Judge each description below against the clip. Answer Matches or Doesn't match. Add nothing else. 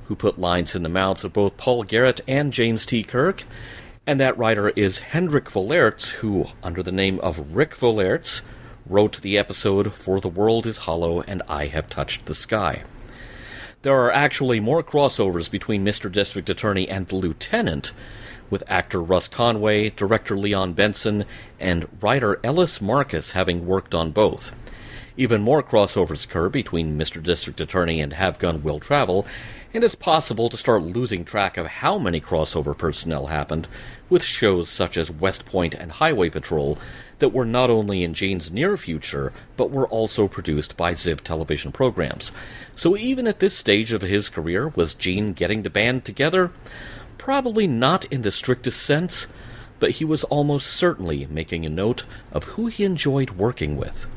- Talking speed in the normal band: Matches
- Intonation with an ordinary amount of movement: Doesn't match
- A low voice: Matches